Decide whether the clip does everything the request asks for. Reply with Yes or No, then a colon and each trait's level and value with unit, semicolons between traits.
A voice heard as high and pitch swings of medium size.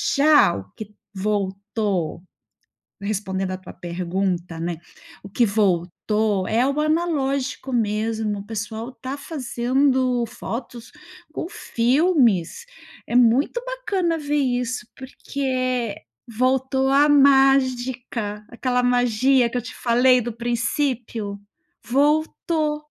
Yes: high, 245 Hz; average, 4.3 semitones